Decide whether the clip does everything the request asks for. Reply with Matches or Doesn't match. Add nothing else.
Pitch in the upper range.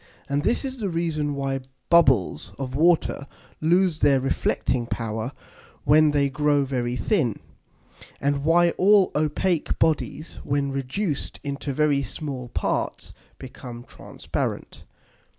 Doesn't match